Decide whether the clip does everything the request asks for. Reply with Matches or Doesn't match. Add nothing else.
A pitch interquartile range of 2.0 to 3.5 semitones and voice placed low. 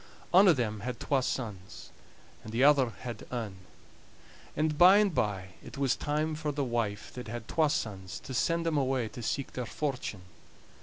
Doesn't match